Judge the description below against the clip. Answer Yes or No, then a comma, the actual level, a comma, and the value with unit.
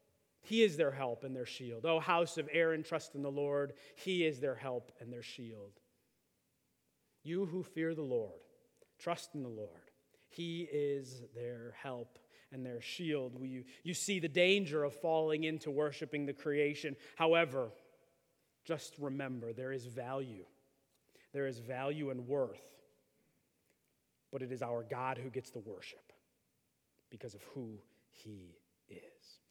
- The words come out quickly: No, average, 150 wpm